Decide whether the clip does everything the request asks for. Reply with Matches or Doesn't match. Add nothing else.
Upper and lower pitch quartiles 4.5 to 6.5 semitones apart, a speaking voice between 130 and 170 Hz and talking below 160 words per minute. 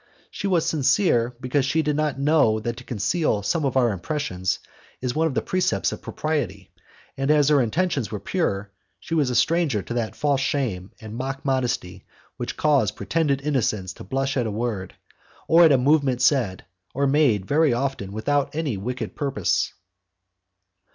Doesn't match